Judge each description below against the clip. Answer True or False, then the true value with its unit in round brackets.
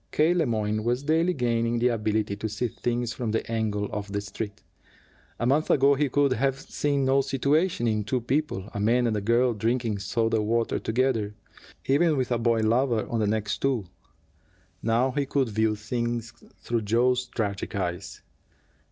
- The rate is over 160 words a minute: True (180 wpm)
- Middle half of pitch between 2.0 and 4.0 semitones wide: True (3.4 semitones)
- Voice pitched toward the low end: True (115 Hz)